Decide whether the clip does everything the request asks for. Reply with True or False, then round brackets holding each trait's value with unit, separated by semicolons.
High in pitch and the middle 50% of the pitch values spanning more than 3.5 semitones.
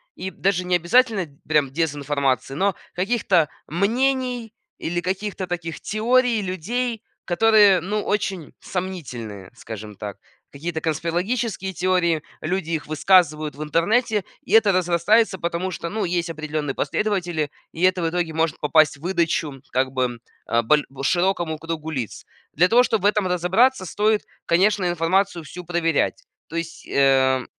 False (175 Hz; 4.2 semitones)